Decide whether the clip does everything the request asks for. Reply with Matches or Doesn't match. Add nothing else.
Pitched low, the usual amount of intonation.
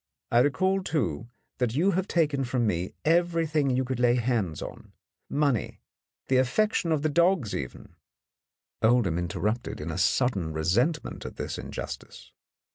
Doesn't match